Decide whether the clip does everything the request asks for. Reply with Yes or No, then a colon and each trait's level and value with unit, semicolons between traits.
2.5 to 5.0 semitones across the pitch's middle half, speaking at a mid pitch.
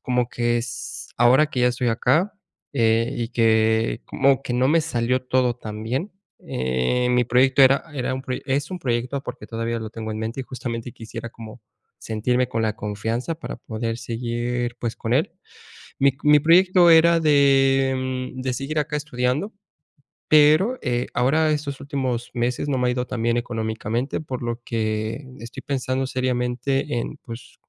No: average, 2.8 semitones; low, 125 Hz